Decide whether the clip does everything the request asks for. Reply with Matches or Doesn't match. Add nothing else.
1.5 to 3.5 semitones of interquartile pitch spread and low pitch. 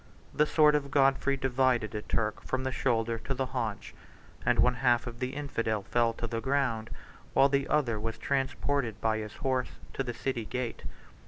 Matches